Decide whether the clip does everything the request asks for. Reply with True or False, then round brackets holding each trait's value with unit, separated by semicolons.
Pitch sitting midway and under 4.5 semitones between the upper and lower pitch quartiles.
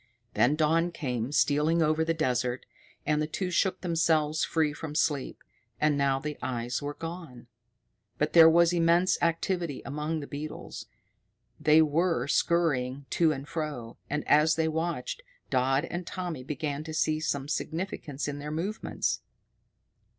True (155 Hz; 2.7 semitones)